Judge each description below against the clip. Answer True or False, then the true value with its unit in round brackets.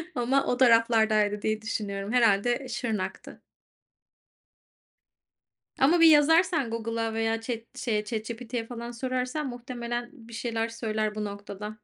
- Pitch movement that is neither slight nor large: False (2.3 semitones)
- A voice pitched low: False (230 Hz)